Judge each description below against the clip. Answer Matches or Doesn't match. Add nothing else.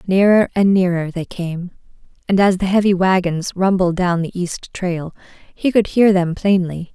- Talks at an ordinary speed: Matches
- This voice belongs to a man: Doesn't match